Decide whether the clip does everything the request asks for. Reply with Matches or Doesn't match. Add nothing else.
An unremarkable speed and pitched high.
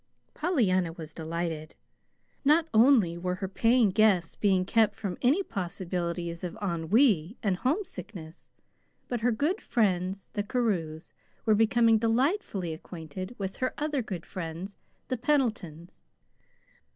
Doesn't match